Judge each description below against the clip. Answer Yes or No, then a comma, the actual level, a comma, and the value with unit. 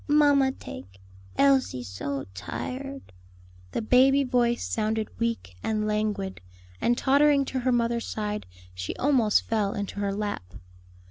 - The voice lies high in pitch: Yes, high, 225 Hz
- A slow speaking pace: Yes, slow, 130 wpm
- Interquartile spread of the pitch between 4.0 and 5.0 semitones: Yes, average, 4.7 semitones